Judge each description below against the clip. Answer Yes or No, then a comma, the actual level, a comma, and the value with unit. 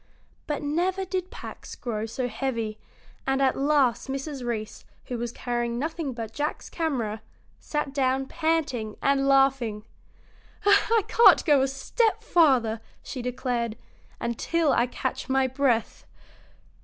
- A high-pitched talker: Yes, very high, 265 Hz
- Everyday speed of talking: No, slow, 130 wpm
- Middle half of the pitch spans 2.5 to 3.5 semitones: No, average, 3.9 semitones